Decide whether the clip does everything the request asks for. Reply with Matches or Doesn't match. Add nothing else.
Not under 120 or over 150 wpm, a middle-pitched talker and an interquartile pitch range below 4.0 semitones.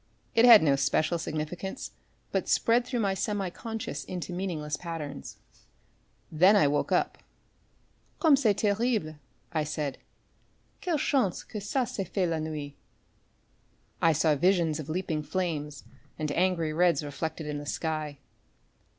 Doesn't match